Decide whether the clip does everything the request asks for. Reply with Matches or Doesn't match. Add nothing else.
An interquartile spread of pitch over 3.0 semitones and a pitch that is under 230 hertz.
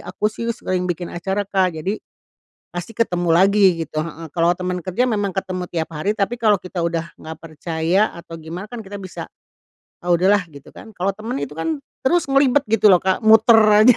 Matches